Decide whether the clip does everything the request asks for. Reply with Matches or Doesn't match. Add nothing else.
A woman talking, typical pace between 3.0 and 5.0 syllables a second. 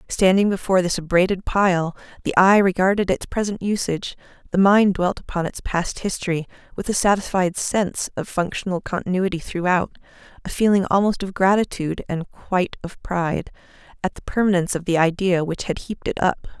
Doesn't match